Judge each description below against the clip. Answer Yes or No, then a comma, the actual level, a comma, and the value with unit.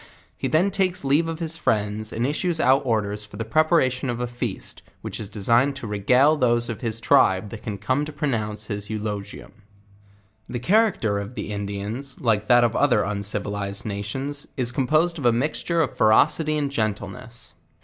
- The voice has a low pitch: Yes, low, 120 Hz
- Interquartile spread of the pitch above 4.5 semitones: Yes, wide, 5.5 semitones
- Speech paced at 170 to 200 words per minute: Yes, average, 190 wpm